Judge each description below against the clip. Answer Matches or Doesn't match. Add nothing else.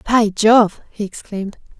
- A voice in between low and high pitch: Doesn't match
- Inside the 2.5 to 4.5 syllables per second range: Matches